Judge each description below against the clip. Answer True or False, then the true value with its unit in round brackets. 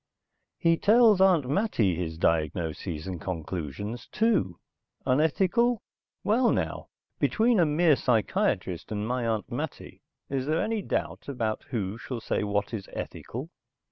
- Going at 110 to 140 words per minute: True (135 wpm)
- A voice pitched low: True (125 Hz)